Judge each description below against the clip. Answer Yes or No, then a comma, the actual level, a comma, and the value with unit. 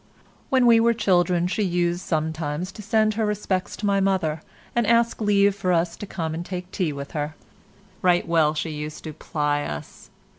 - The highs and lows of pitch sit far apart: No, average, 4.5 semitones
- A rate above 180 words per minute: Yes, average, 190 wpm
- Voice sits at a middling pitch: Yes, medium, 180 Hz